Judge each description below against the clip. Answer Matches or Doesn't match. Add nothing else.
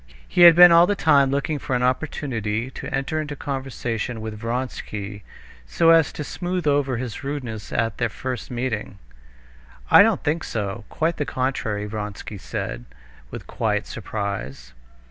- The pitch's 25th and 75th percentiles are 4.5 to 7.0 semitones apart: Matches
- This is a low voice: Matches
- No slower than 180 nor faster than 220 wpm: Doesn't match